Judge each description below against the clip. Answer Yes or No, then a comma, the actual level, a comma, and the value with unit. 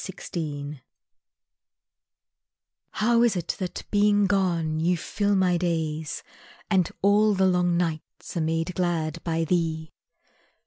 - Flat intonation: No, average, 3.0 semitones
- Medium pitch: Yes, medium, 175 Hz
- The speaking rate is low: Yes, slow, 120 wpm